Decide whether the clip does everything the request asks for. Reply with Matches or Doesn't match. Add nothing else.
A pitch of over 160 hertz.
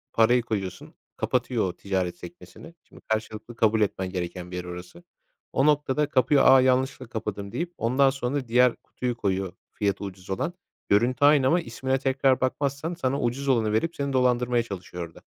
Doesn't match